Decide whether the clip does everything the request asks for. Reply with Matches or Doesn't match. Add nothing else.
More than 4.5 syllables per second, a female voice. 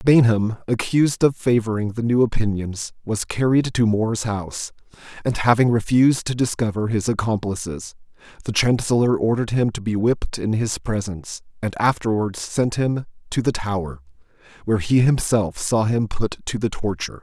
Doesn't match